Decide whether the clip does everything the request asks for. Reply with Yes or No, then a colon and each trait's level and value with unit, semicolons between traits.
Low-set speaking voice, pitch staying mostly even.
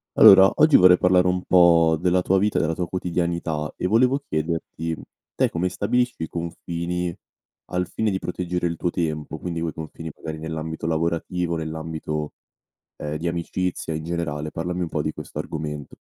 Yes: very low, 85 Hz; narrow, 2.2 semitones